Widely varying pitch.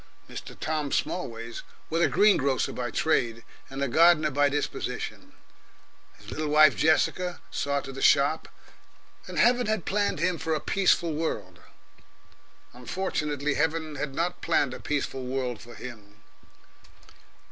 No: average, 3.8 semitones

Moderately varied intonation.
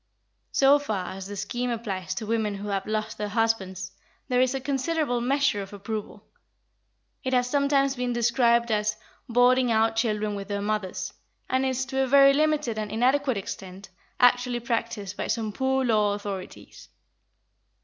Yes: average, 3.9 semitones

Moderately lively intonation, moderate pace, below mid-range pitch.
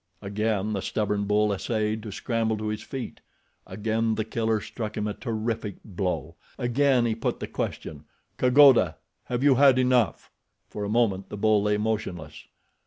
No: narrow, 2.2 semitones; average, 160 wpm; low, 110 Hz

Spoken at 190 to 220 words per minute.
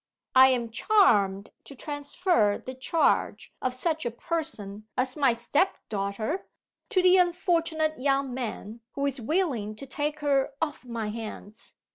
No: average, 145 wpm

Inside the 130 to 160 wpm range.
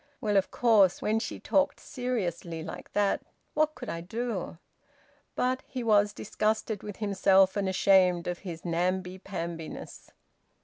Yes: average, 140 wpm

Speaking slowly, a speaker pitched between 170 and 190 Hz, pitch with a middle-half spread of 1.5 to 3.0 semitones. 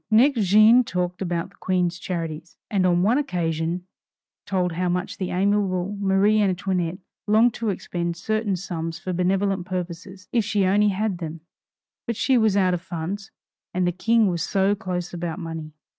No: average, 170 wpm; medium, 185 Hz; average, 2.7 semitones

